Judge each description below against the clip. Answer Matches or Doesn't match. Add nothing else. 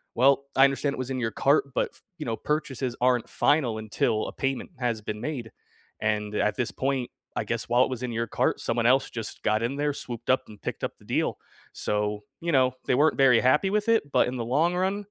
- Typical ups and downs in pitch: Matches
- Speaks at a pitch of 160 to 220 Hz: Doesn't match